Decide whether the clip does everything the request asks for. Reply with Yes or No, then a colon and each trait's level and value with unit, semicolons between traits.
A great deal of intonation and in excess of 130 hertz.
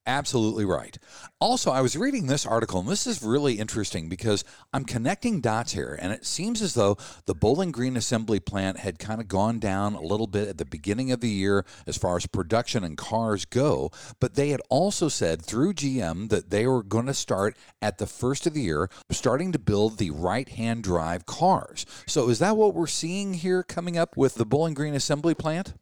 No: wide, 6.1 semitones; low, 120 Hz